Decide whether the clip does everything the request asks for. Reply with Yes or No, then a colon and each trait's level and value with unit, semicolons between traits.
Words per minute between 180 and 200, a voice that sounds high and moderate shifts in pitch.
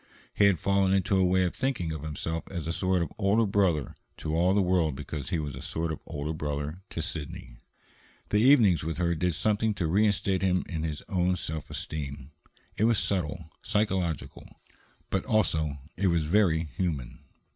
No: average, 185 wpm; very low, 85 Hz; average, 3.9 semitones